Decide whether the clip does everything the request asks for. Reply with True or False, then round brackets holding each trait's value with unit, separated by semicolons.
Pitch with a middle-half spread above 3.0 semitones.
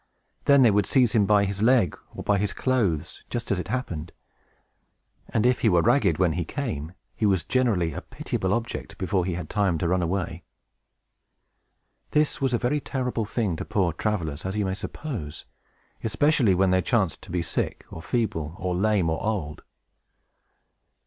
True (5.2 semitones)